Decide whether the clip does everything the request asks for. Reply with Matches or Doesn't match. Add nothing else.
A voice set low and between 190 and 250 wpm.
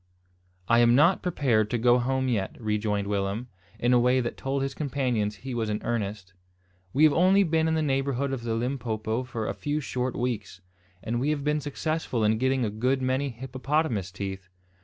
Matches